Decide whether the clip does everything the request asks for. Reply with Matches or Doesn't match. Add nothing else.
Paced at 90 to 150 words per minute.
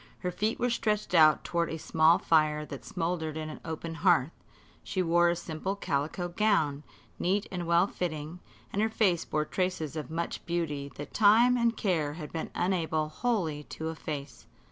Doesn't match